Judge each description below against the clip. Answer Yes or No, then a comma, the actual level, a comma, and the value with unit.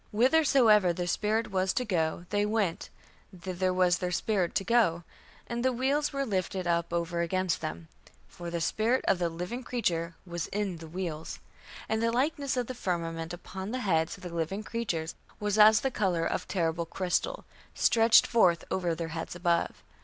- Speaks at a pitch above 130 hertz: Yes, medium, 185 Hz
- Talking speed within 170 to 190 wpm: Yes, average, 180 wpm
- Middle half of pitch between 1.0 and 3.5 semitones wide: No, average, 4.8 semitones